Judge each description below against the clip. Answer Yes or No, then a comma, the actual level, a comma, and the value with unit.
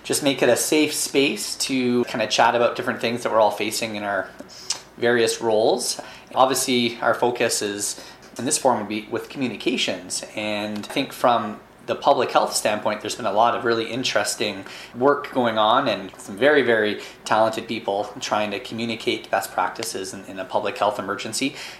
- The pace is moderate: Yes, average, 185 wpm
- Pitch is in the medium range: No, low, 115 Hz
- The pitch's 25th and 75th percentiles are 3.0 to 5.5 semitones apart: No, narrow, 2.5 semitones